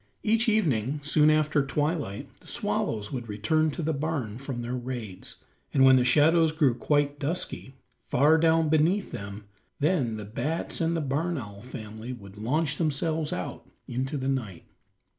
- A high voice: No, medium, 140 Hz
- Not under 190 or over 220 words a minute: No, average, 160 wpm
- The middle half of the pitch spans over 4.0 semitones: Yes, average, 4.8 semitones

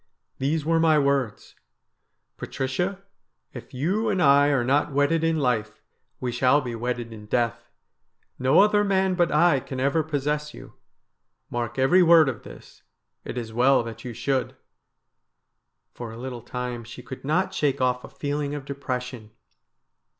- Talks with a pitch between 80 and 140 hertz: Yes, low, 135 Hz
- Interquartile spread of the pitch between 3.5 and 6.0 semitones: Yes, average, 3.9 semitones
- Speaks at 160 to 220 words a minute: Yes, average, 170 wpm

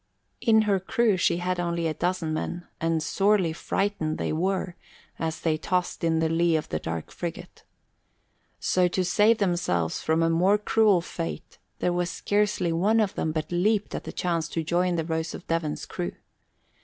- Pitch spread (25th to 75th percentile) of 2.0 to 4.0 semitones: Yes, average, 2.8 semitones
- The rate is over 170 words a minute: Yes, average, 180 wpm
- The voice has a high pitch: No, medium, 175 Hz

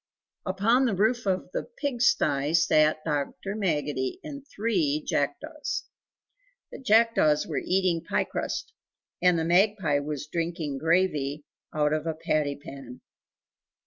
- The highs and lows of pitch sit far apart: Yes, wide, 6.1 semitones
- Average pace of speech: No, slow, 130 wpm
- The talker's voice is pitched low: No, medium, 165 Hz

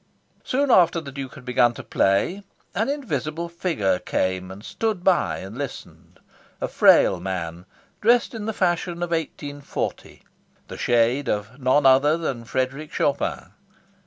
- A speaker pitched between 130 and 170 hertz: Yes, medium, 140 Hz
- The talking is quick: No, average, 145 wpm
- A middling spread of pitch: No, wide, 6.9 semitones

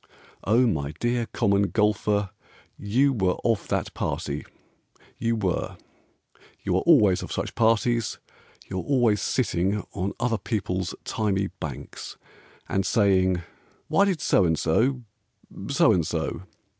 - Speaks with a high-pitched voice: No, low, 100 Hz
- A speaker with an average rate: No, slow, 130 wpm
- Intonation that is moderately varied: Yes, average, 3.8 semitones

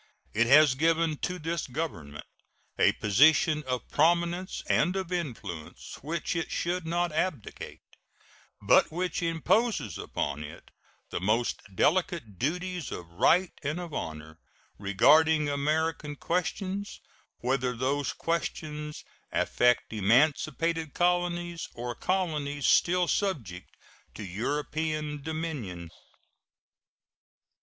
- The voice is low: No, medium, 155 Hz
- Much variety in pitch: Yes, wide, 5.7 semitones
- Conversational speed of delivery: No, slow, 105 wpm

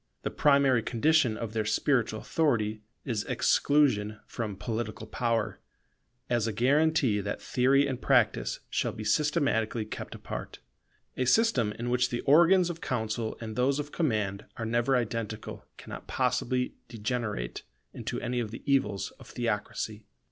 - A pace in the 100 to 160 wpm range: Yes, average, 145 wpm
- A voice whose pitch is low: Yes, low, 120 Hz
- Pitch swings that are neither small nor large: Yes, average, 4.1 semitones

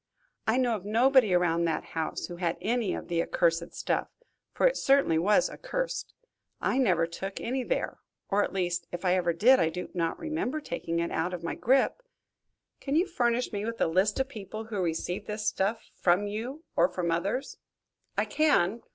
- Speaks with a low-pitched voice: No, high, 205 Hz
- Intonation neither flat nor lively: No, wide, 6.3 semitones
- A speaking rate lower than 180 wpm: No, average, 195 wpm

